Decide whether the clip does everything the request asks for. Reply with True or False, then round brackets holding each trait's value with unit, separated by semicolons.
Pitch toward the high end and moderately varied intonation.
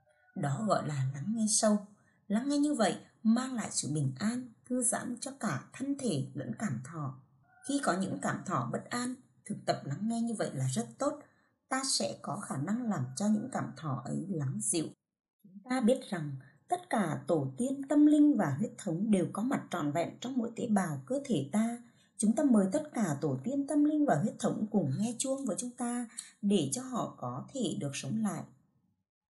False (220 Hz; 7.0 semitones)